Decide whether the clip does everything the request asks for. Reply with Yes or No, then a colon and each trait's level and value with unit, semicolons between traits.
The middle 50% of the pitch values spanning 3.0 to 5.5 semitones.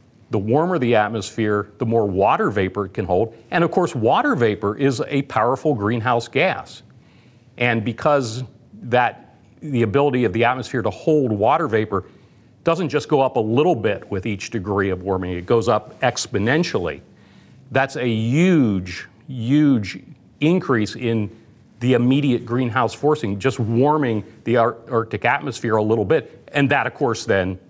Yes: average, 3.7 semitones